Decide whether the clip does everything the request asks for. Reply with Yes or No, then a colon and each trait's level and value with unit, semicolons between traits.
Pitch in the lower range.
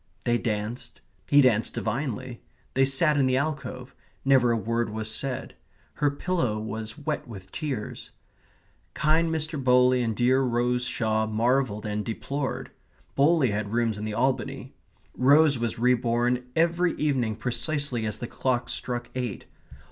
Yes: low, 125 Hz